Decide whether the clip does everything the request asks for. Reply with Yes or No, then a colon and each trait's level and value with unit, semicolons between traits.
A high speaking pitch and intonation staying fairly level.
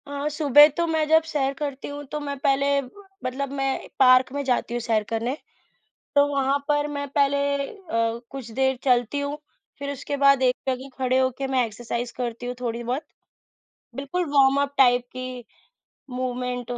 Yes: very high, 270 Hz; narrow, 2.3 semitones